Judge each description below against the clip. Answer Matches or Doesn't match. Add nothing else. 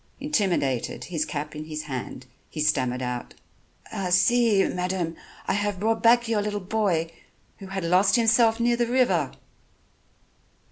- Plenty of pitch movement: Matches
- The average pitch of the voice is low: Doesn't match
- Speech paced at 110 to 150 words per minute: Matches